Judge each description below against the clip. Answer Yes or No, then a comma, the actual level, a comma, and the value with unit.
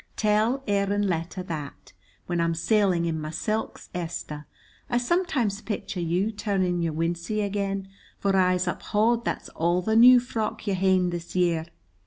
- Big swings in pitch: No, average, 3.8 semitones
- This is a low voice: No, high, 190 Hz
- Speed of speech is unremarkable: Yes, average, 155 wpm